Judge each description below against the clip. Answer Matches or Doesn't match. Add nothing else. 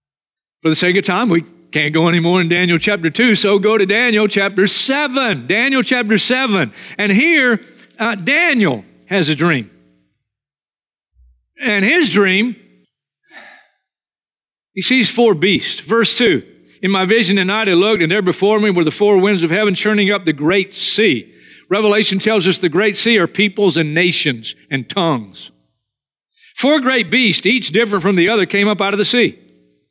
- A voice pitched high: Matches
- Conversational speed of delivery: Matches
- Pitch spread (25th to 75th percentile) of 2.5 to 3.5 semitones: Doesn't match